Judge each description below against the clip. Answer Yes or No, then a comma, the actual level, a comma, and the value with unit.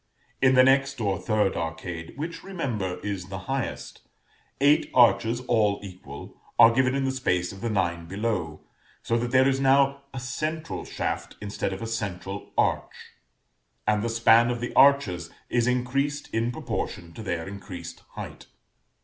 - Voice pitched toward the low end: Yes, low, 115 Hz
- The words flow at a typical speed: Yes, average, 160 wpm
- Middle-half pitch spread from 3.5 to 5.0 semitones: No, wide, 5.4 semitones